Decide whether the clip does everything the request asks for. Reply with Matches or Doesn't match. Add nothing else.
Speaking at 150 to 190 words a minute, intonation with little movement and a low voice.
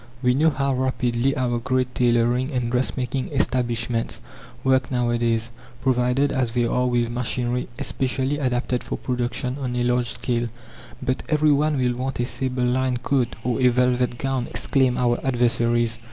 Matches